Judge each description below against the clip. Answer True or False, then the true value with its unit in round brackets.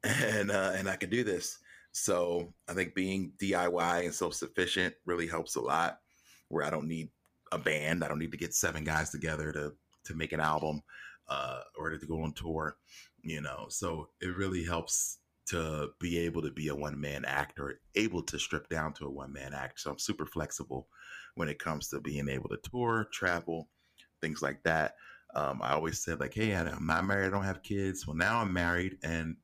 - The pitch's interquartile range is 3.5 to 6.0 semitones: False (3.1 semitones)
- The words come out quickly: True (210 wpm)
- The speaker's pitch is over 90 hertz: False (80 Hz)